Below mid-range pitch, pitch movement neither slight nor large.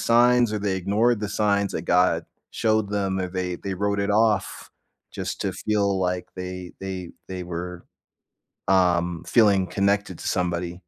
No: very low, 95 Hz; narrow, 2.3 semitones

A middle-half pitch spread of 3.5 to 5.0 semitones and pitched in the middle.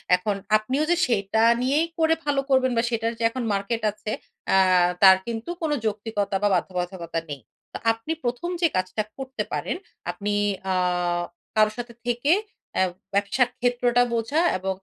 No: average, 4.0 semitones; high, 225 Hz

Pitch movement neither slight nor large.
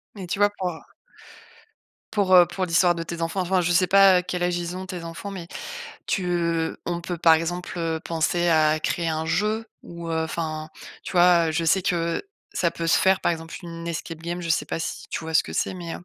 No: narrow, 1.5 semitones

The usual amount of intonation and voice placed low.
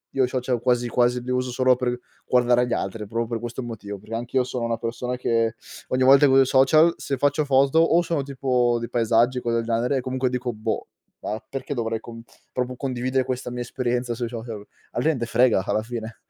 No: narrow, 1.9 semitones; low, 125 Hz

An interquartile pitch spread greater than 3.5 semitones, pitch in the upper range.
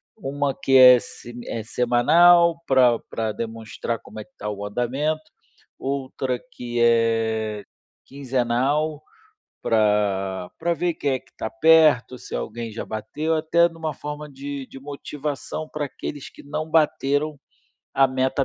No: average, 4.6 semitones; low, 130 Hz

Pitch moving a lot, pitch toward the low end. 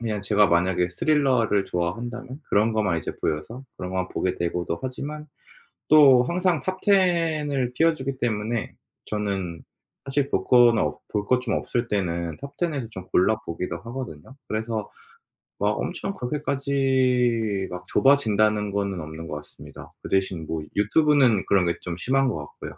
Yes: wide, 6.2 semitones; low, 115 Hz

